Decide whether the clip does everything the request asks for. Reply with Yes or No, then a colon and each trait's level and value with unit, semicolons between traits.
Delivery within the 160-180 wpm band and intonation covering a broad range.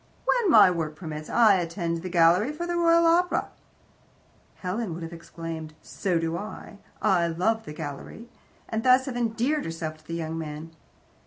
Yes: average, 170 wpm; wide, 6.1 semitones